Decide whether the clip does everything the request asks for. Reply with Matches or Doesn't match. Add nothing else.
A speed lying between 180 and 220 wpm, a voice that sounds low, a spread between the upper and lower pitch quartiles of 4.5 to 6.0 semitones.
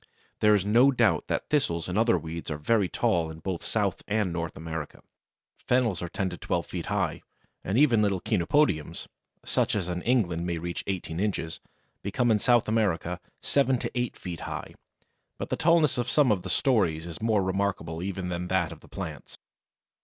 Matches